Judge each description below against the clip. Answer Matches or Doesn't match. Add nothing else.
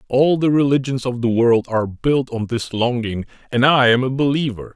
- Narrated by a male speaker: Matches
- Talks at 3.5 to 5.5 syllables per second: Matches